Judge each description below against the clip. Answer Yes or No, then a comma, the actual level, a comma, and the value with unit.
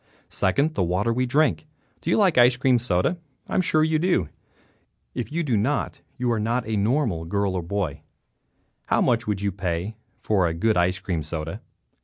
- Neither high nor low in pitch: No, low, 110 Hz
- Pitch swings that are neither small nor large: No, wide, 5.9 semitones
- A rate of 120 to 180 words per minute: No, fast, 205 wpm